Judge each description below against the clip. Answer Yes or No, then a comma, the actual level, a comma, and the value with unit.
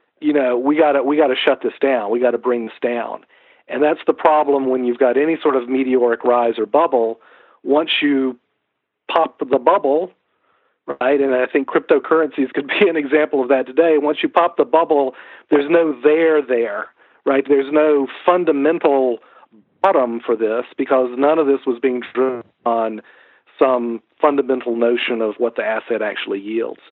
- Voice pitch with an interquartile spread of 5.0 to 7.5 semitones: No, average, 3.7 semitones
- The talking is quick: No, average, 180 wpm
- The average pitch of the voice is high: No, low, 135 Hz